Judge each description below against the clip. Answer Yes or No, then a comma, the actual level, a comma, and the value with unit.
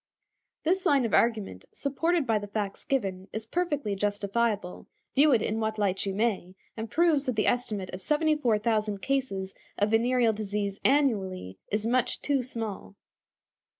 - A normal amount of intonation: Yes, average, 4.7 semitones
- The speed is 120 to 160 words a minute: Yes, average, 150 wpm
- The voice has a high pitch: Yes, high, 220 Hz